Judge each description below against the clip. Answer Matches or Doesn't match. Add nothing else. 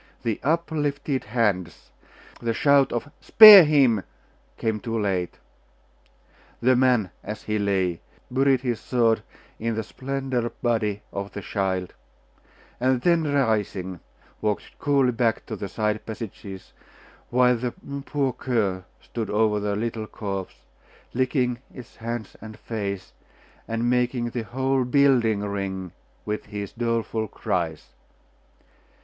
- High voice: Doesn't match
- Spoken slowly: Matches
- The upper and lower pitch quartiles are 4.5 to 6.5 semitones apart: Doesn't match